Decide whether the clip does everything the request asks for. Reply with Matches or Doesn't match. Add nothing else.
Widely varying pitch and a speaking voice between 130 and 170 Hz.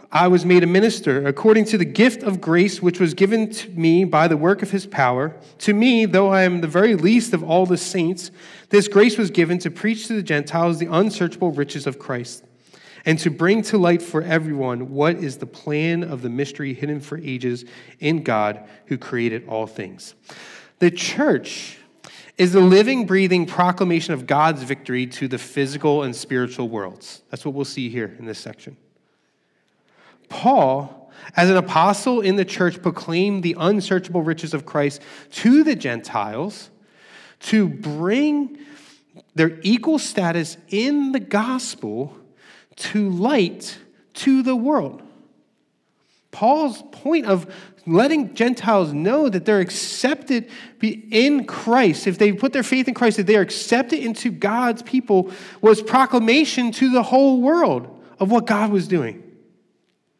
Doesn't match